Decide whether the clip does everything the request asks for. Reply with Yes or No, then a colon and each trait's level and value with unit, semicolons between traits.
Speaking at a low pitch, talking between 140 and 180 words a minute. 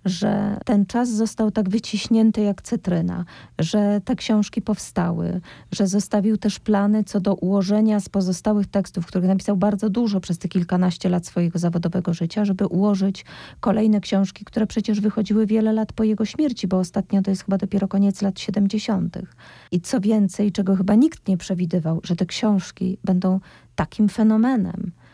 No: high, 200 Hz; fast, 160 wpm